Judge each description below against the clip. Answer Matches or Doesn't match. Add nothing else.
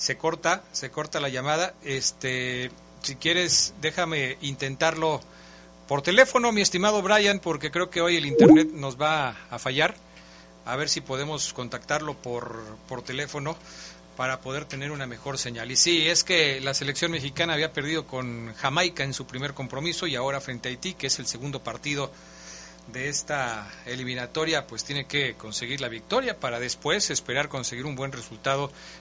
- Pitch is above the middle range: Doesn't match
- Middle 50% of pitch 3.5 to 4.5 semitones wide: Matches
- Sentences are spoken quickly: Doesn't match